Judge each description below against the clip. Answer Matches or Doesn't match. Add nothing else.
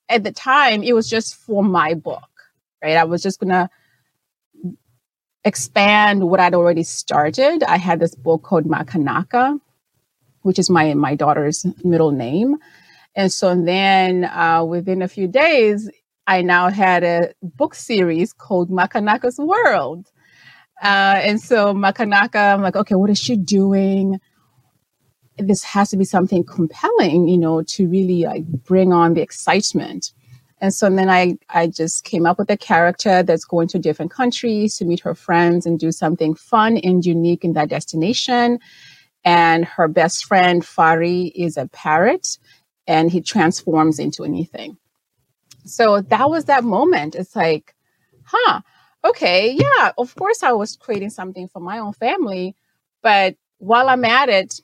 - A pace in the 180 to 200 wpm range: Doesn't match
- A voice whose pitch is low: Doesn't match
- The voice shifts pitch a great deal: Doesn't match